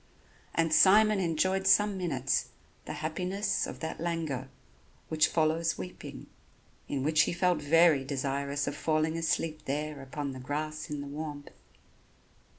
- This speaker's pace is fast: No, average, 140 wpm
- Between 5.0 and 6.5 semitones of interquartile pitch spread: No, average, 2.9 semitones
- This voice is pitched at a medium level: Yes, medium, 155 Hz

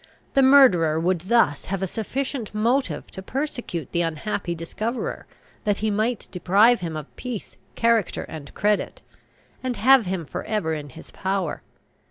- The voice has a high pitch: Yes, high, 200 Hz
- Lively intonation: Yes, wide, 5.8 semitones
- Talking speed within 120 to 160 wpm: Yes, average, 155 wpm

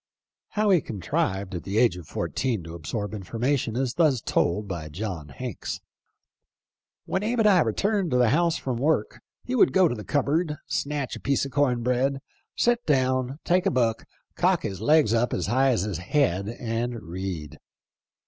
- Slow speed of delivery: No, average, 180 wpm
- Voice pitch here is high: No, low, 125 Hz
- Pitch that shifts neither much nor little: No, wide, 6.7 semitones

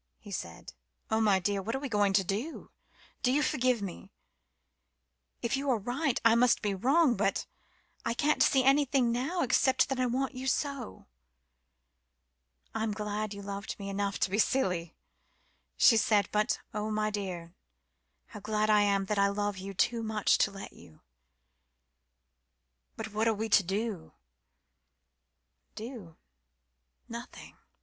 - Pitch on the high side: Yes, high, 215 Hz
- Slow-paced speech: No, average, 150 wpm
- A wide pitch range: No, average, 3.8 semitones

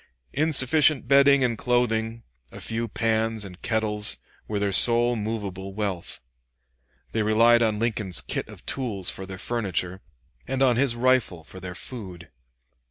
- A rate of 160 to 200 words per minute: No, average, 145 wpm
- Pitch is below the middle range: Yes, low, 110 Hz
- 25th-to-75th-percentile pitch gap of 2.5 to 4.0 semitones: Yes, average, 3.6 semitones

